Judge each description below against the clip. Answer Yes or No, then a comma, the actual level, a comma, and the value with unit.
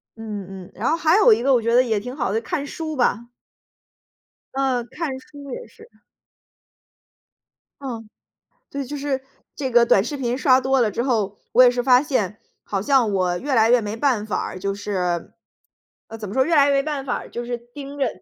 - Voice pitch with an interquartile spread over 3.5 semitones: Yes, average, 4.2 semitones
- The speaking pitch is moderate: No, high, 245 Hz